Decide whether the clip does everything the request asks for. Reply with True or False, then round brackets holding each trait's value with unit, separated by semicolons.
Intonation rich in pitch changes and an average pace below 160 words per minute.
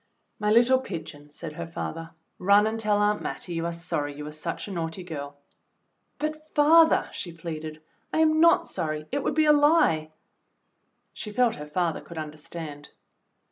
False (7.0 semitones; 175 wpm)